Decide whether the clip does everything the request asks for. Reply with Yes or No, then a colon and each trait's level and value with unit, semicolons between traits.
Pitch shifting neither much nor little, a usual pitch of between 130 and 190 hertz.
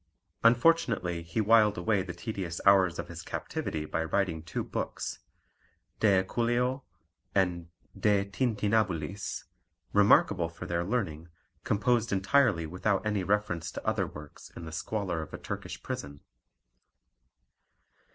No: average, 4.2 semitones; very low, 95 Hz